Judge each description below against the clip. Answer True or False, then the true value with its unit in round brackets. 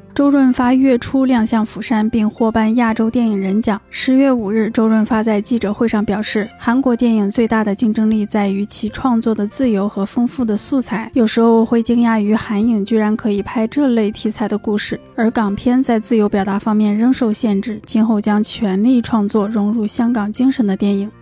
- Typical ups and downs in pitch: False (2.2 semitones)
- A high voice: True (220 Hz)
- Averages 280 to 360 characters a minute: True (305 characters per minute)